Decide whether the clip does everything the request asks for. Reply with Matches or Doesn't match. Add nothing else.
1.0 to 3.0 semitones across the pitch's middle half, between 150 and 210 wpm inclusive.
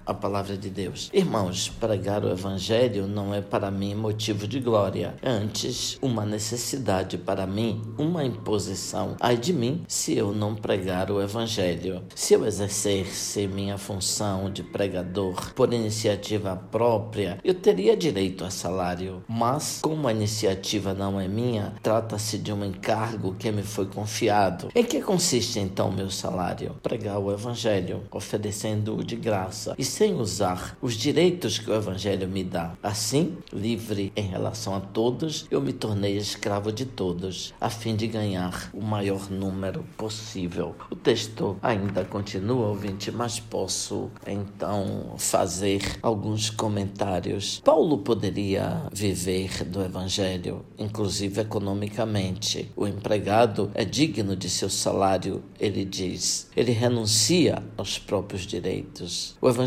Doesn't match